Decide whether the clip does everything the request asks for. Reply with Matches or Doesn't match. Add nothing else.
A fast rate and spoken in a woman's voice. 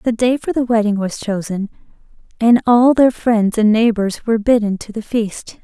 Doesn't match